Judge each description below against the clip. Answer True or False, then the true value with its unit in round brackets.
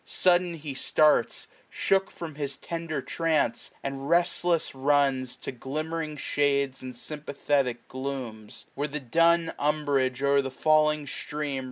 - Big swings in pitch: False (2.7 semitones)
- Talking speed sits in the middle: False (130 wpm)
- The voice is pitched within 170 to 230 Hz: False (145 Hz)